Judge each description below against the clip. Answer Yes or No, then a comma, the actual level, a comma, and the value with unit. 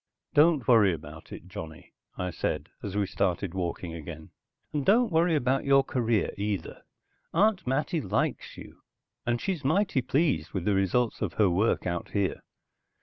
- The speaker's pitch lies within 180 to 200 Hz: No, low, 110 Hz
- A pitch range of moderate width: No, wide, 8.1 semitones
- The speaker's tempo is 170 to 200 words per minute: No, average, 160 wpm